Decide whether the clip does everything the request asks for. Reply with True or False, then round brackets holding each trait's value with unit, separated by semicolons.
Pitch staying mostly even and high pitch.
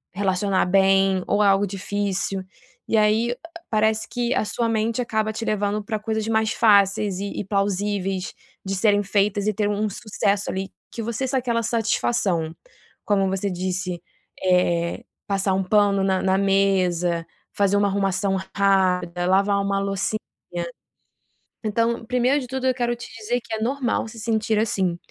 True (2.3 semitones; 205 Hz)